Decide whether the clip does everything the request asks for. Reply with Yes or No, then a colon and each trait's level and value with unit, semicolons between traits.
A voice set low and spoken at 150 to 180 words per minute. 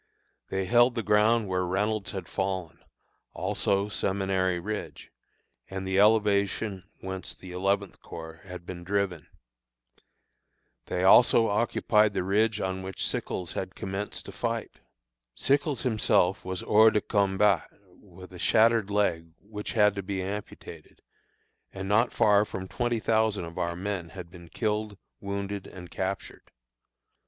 No: low, 100 Hz; average, 140 wpm